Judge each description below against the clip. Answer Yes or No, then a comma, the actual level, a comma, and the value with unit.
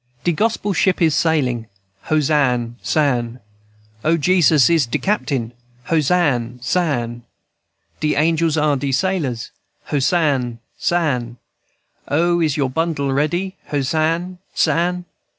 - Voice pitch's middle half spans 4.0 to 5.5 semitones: Yes, average, 4.7 semitones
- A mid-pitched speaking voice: Yes, medium, 150 Hz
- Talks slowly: Yes, slow, 115 wpm